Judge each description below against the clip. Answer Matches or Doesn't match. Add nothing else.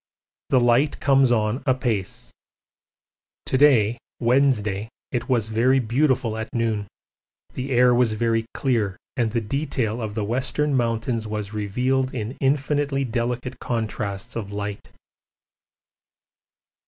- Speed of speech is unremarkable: Doesn't match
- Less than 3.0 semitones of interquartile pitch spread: Doesn't match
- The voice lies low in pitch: Matches